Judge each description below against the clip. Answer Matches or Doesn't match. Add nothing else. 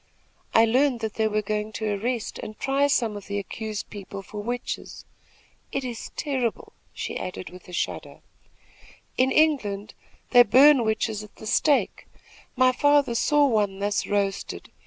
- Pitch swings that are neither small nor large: Matches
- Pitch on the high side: Matches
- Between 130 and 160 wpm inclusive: Matches